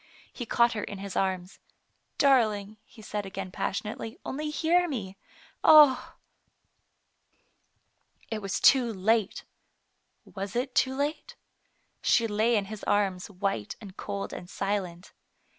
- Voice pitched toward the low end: No, high, 210 Hz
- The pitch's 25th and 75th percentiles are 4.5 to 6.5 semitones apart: No, average, 3.9 semitones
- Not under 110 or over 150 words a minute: Yes, average, 140 wpm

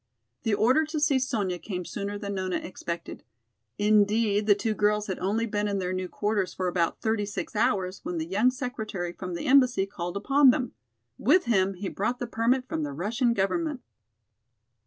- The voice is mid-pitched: No, high, 205 Hz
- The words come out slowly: No, average, 185 wpm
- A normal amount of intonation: Yes, average, 4.2 semitones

